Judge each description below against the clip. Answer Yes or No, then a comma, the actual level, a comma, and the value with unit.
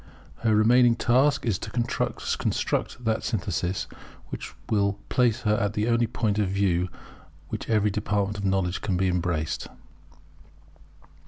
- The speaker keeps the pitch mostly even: No, average, 3.2 semitones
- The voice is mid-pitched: No, low, 105 Hz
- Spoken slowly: No, average, 145 wpm